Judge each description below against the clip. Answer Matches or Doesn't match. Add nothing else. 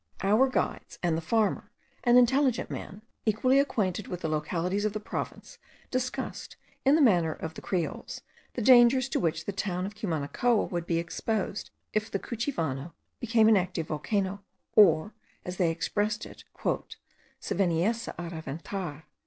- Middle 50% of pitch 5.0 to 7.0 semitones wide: Matches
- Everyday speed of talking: Matches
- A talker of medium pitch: Doesn't match